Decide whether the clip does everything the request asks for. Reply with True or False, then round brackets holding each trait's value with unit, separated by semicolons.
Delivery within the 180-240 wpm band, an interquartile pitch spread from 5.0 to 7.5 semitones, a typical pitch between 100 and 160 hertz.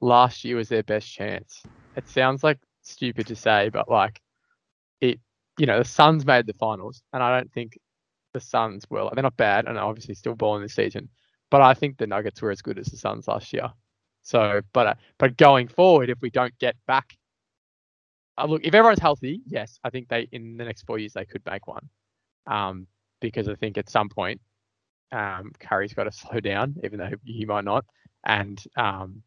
False (205 wpm; 3.7 semitones; 115 Hz)